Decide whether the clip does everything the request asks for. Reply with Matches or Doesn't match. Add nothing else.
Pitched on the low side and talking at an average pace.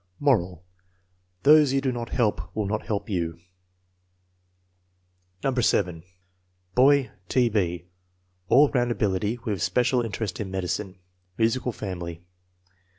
Doesn't match